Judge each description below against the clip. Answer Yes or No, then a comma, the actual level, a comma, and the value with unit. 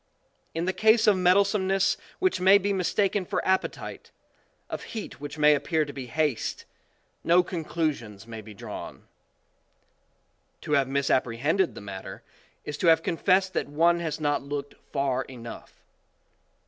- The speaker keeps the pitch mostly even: No, average, 5.3 semitones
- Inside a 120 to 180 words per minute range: Yes, average, 155 wpm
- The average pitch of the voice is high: No, medium, 160 Hz